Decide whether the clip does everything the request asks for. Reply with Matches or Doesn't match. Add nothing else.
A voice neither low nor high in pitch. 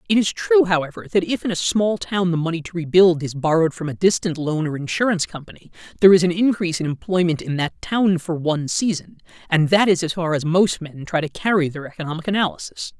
Matches